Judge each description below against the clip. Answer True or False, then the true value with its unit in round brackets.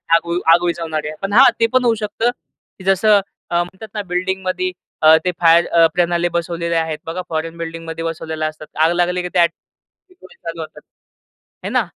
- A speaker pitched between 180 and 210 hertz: False (170 Hz)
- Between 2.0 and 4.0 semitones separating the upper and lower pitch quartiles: True (2.5 semitones)